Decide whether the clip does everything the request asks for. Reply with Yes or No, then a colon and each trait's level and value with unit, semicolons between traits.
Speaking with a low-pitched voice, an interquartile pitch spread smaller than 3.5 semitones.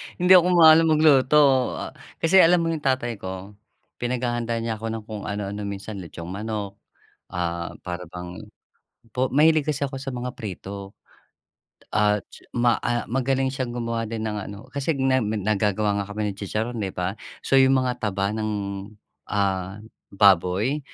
No: low, 110 Hz; average, 4.8 semitones